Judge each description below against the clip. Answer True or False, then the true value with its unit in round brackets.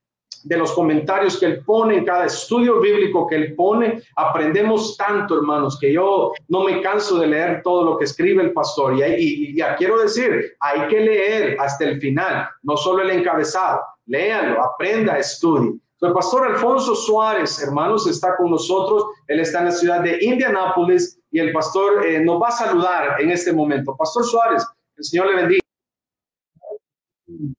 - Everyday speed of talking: True (175 wpm)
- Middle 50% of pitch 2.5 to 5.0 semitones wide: False (5.5 semitones)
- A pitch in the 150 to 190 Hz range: True (185 Hz)